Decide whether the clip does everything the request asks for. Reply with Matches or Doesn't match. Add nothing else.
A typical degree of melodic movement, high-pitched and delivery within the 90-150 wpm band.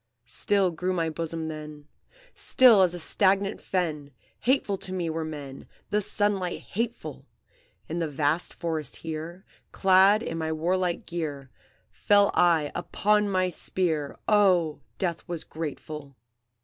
Doesn't match